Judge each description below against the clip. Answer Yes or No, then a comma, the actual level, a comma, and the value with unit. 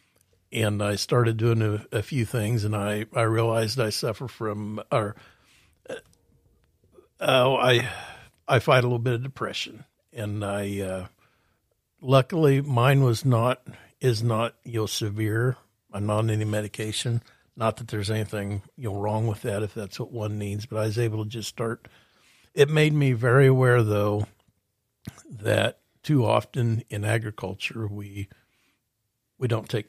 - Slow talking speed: No, average, 160 wpm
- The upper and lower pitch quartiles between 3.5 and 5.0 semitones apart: No, narrow, 2.6 semitones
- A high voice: No, low, 115 Hz